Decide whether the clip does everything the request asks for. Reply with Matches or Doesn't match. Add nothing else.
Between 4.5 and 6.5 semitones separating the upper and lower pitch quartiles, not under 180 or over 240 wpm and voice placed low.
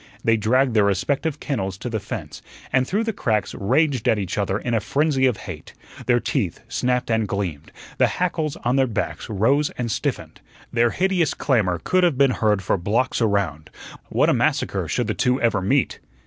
Matches